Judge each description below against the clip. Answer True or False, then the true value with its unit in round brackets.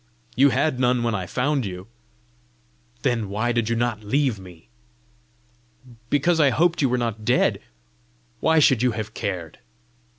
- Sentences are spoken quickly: False (155 wpm)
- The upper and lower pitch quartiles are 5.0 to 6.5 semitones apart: False (4.4 semitones)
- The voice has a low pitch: True (120 Hz)